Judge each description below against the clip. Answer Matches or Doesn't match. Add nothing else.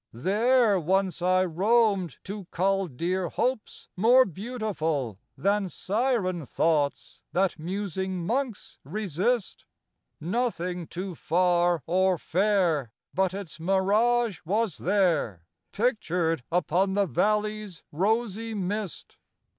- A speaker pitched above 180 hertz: Matches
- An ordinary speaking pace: Doesn't match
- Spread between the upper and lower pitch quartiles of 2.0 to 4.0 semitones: Matches